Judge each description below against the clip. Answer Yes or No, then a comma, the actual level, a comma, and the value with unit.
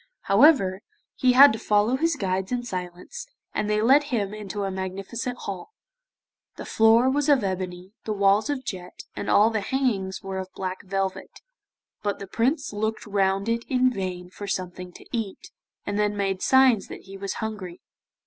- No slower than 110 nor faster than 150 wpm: No, average, 175 wpm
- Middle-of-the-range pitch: No, high, 205 Hz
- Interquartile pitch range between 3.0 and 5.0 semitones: Yes, average, 4.0 semitones